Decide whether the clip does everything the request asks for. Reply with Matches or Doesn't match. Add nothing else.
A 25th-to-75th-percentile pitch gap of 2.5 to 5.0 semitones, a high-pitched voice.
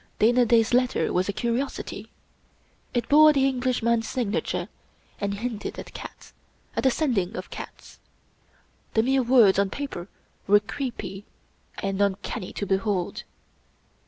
Matches